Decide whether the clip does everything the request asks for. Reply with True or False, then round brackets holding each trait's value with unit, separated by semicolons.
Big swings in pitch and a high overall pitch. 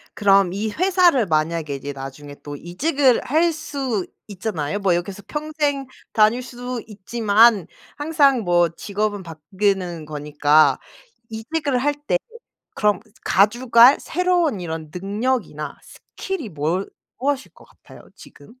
True (7.5 semitones; 210 Hz)